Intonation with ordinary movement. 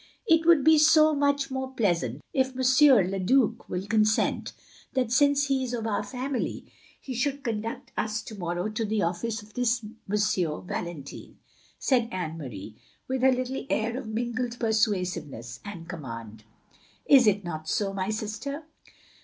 No: wide, 5.9 semitones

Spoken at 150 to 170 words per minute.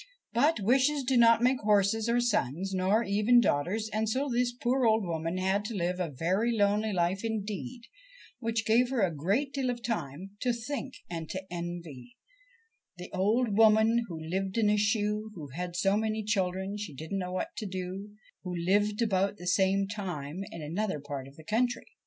No: average, 190 wpm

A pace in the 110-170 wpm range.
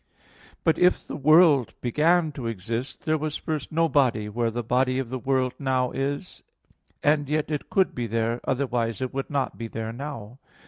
No: average, 185 wpm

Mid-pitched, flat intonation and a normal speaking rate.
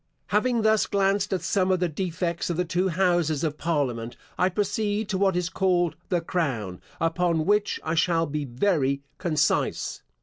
No: medium, 175 Hz; average, 3.5 semitones; average, 170 wpm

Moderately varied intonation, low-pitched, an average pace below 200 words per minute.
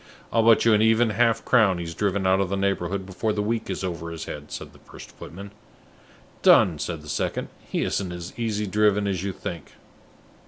No: average, 3.4 semitones; low, 100 Hz; fast, 205 wpm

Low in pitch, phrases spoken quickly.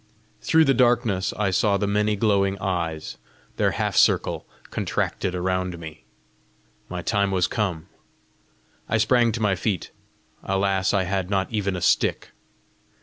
No: low, 100 Hz; average, 145 wpm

